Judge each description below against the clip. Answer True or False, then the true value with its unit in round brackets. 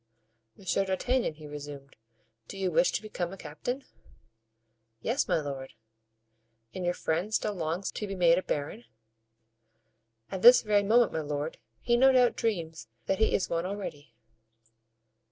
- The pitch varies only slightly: False (5.3 semitones)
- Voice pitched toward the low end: False (185 Hz)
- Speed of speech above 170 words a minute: False (155 wpm)